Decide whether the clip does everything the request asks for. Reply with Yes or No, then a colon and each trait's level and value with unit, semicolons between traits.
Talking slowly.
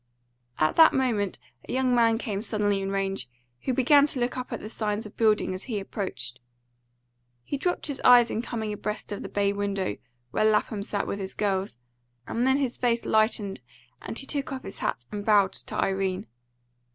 No: average, 195 wpm